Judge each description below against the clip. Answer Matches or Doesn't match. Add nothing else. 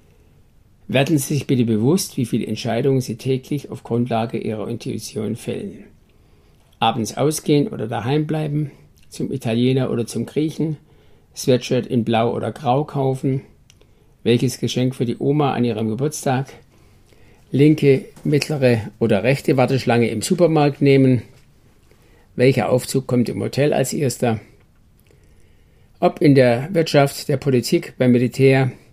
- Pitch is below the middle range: Matches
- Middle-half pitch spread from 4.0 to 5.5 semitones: Doesn't match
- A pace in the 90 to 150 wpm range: Matches